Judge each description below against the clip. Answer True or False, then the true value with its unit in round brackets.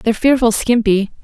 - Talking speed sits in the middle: True (145 wpm)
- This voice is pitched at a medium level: False (225 Hz)